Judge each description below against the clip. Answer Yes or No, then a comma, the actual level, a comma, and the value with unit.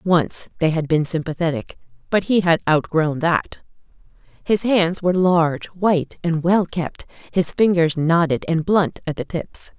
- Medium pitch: Yes, medium, 170 Hz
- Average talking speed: Yes, average, 160 wpm